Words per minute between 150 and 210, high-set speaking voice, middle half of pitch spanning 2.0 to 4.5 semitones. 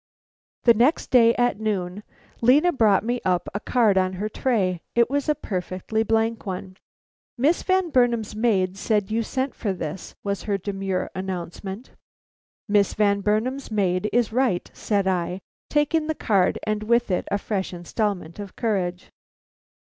Yes: average, 155 wpm; high, 210 Hz; average, 4.0 semitones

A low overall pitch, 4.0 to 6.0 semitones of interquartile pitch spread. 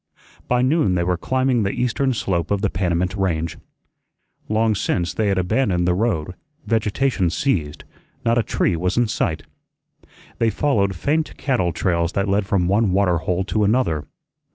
Yes: low, 100 Hz; average, 4.6 semitones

